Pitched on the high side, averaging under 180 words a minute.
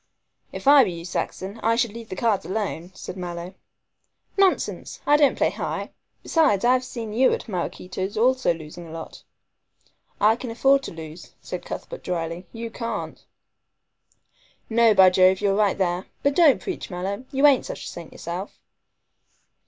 Yes: high, 205 Hz; average, 165 wpm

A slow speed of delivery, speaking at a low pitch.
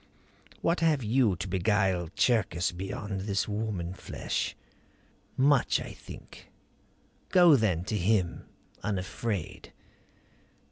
Yes: slow, 100 wpm; low, 105 Hz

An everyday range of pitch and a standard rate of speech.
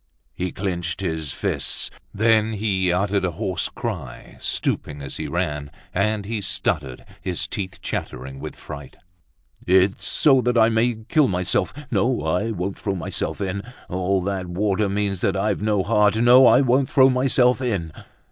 Yes: average, 3.8 semitones; average, 160 wpm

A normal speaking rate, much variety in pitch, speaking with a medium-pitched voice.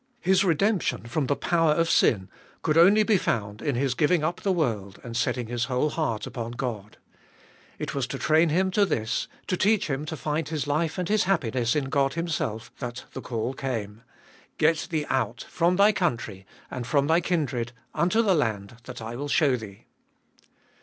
Yes: average, 190 wpm; wide, 6.1 semitones; medium, 145 Hz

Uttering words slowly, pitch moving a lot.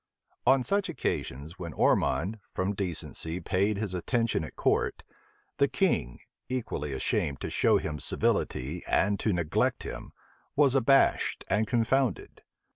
Yes: slow, 130 wpm; wide, 6.7 semitones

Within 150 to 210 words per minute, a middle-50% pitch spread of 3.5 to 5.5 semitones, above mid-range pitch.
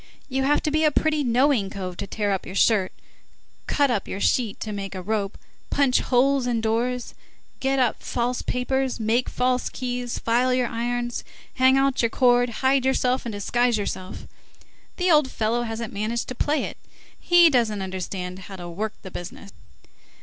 Yes: average, 180 wpm; average, 3.8 semitones; high, 240 Hz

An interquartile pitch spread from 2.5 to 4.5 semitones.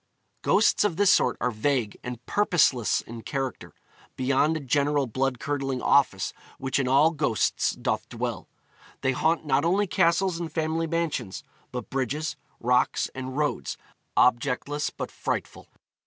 Yes: average, 4.1 semitones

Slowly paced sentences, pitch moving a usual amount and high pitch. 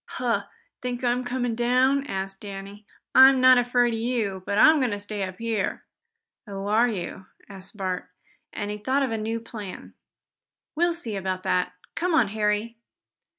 No: average, 170 wpm; average, 3.9 semitones; high, 225 Hz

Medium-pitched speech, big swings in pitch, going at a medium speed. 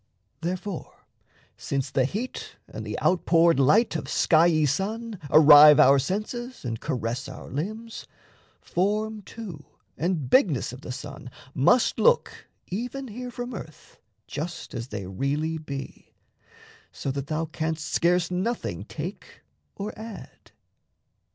No: medium, 165 Hz; wide, 7.2 semitones; slow, 125 wpm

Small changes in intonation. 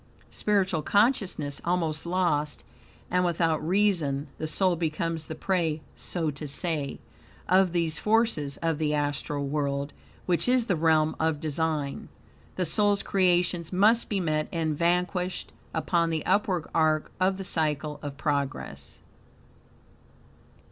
No: average, 3.3 semitones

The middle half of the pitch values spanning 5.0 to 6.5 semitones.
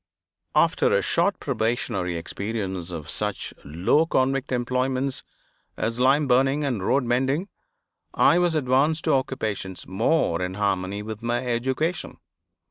Yes: average, 5.3 semitones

